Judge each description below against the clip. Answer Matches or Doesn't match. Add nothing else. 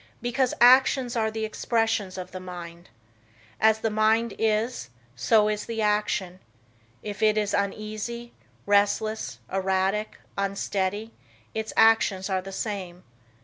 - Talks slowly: Matches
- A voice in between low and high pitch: Doesn't match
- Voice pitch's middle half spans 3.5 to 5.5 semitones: Doesn't match